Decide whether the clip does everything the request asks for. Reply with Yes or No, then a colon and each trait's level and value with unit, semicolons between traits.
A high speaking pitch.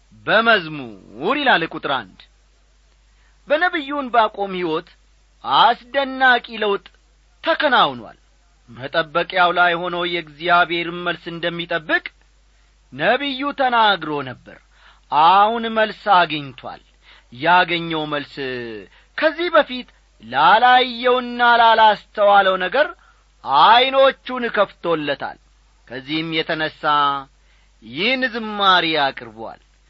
No: medium, 180 Hz